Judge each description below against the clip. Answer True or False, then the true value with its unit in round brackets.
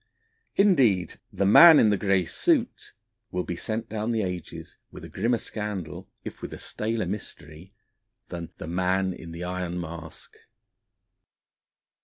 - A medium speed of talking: True (145 wpm)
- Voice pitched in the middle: False (95 Hz)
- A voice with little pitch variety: False (3.9 semitones)